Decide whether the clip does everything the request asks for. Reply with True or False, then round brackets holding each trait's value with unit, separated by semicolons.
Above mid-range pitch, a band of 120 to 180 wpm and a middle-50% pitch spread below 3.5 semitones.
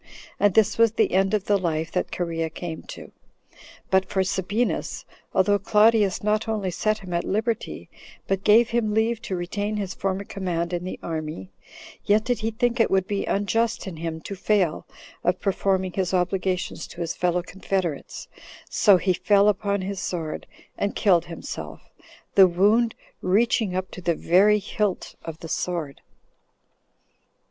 True (195 Hz; 165 wpm; 3.0 semitones)